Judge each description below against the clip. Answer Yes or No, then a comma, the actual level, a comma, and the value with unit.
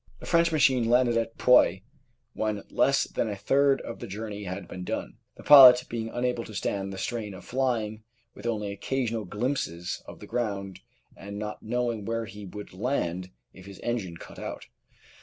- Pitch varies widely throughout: No, average, 3.7 semitones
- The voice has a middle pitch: No, low, 110 Hz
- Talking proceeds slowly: No, average, 180 wpm